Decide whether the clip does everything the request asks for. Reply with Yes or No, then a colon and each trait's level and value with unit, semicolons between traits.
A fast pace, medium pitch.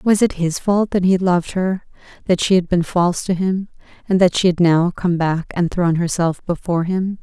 Yes: fast, 235 wpm; medium, 180 Hz